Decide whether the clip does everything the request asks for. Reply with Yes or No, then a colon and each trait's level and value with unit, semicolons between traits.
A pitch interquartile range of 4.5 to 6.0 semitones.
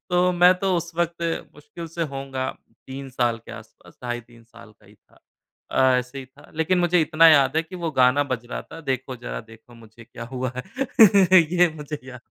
Yes: wide, 5.5 semitones